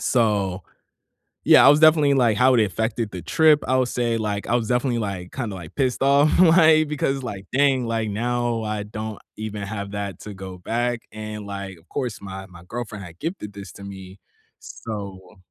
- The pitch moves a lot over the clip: No, average, 4.1 semitones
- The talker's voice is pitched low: Yes, low, 110 Hz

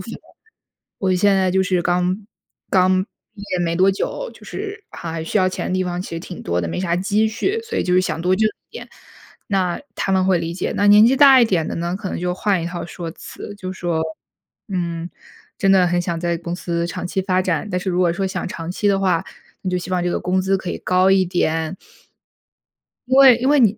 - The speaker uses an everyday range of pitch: No, narrow, 2.0 semitones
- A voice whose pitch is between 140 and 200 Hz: Yes, medium, 185 Hz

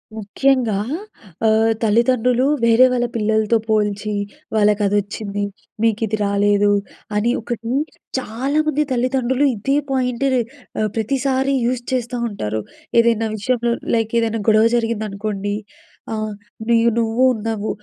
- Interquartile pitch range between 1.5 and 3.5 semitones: Yes, average, 2.8 semitones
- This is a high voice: Yes, high, 225 Hz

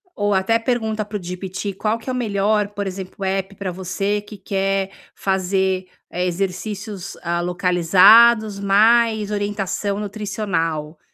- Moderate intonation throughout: No, narrow, 2.1 semitones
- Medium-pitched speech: No, high, 195 Hz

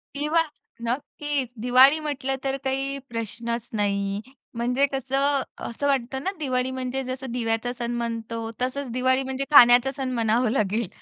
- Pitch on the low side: No, very high, 255 Hz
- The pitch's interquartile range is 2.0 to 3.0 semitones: Yes, narrow, 2.6 semitones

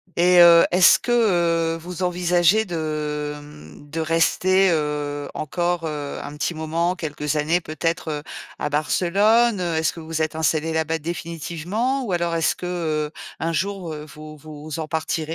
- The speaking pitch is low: No, medium, 165 Hz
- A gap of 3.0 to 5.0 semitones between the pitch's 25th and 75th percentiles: No, narrow, 2.5 semitones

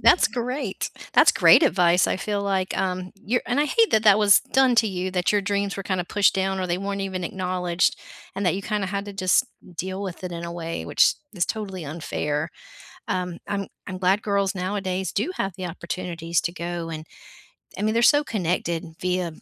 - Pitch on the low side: No, high, 190 Hz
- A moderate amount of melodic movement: No, narrow, 2.3 semitones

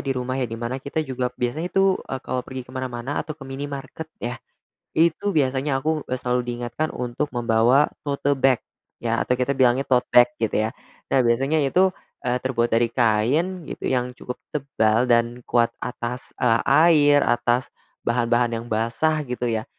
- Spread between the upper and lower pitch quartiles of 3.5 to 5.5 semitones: No, average, 2.9 semitones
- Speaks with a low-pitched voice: Yes, low, 125 Hz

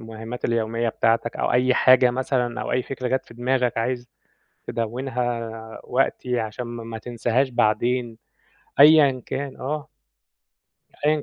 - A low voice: Yes, low, 120 Hz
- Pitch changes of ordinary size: No, narrow, 2.0 semitones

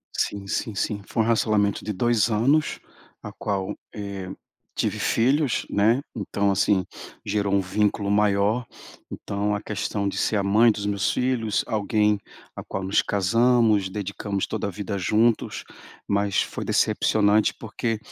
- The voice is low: Yes, low, 105 Hz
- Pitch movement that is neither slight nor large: No, narrow, 2.0 semitones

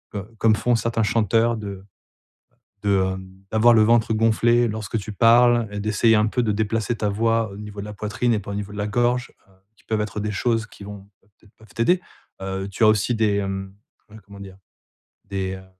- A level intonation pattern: Yes, narrow, 2.1 semitones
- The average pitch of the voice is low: Yes, low, 105 Hz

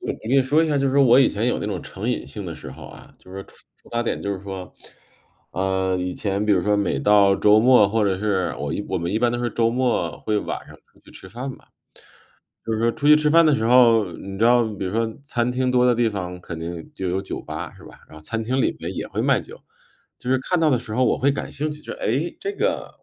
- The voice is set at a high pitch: No, low, 115 Hz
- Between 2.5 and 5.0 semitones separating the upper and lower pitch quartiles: Yes, average, 4.7 semitones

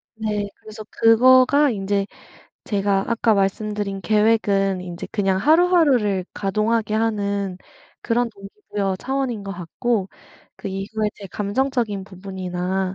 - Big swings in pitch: No, average, 2.7 semitones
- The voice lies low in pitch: No, high, 205 Hz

